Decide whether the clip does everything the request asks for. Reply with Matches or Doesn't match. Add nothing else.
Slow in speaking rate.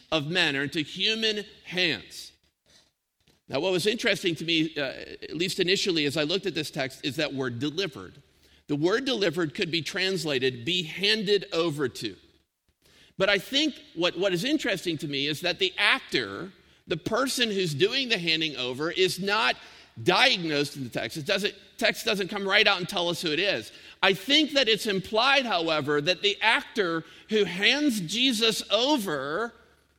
Doesn't match